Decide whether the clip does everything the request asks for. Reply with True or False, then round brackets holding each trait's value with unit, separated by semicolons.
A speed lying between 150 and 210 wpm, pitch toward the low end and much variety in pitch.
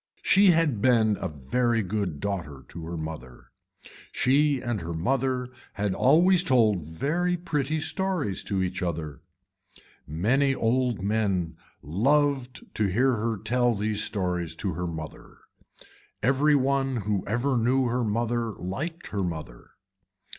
False (135 wpm; 115 Hz; 6.6 semitones)